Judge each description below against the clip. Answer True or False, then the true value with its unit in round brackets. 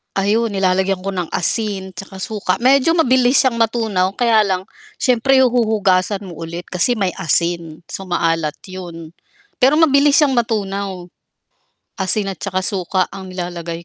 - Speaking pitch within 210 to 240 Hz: False (195 Hz)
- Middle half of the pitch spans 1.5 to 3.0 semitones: False (4.2 semitones)